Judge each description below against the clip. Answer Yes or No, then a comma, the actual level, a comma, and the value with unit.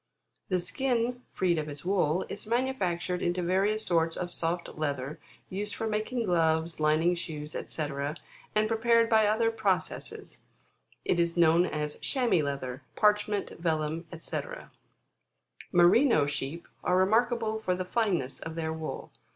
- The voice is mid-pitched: Yes, medium, 180 Hz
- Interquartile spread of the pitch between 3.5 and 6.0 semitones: Yes, average, 5.3 semitones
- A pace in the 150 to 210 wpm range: No, average, 140 wpm